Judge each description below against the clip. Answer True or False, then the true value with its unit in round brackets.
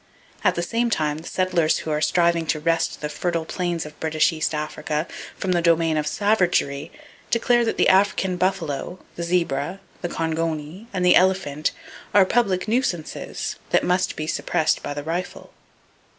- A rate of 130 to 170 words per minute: True (160 wpm)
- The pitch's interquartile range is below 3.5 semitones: True (3.0 semitones)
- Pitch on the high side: False (170 Hz)